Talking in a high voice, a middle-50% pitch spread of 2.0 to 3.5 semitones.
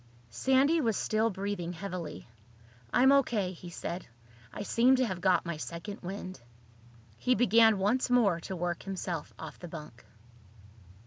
No: high, 195 Hz; average, 4.9 semitones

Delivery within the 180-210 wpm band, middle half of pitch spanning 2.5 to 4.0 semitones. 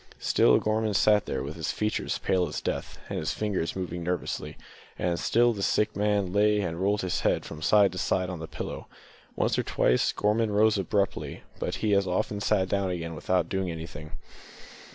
Yes: average, 195 wpm; average, 3.1 semitones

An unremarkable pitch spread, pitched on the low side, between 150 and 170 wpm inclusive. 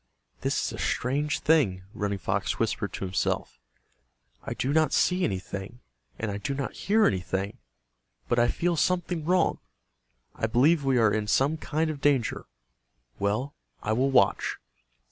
No: wide, 7.0 semitones; low, 130 Hz; average, 155 wpm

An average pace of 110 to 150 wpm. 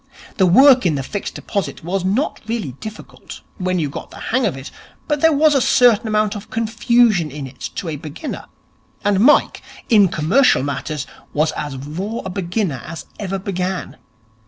No: average, 180 wpm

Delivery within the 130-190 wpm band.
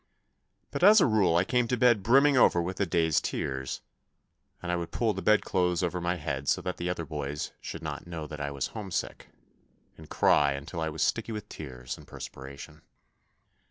No: average, 200 wpm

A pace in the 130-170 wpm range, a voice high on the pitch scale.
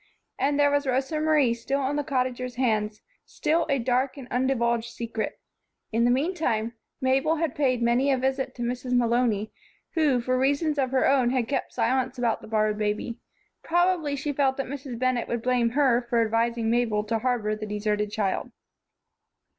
No: average, 180 wpm; very high, 250 Hz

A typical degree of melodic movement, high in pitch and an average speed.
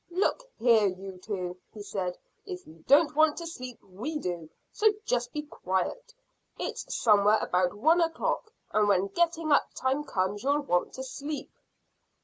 No: wide, 8.3 semitones; high, 240 Hz; average, 160 wpm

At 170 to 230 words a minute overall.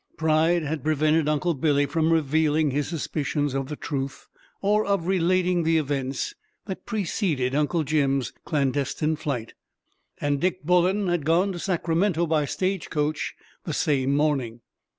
No: average, 145 wpm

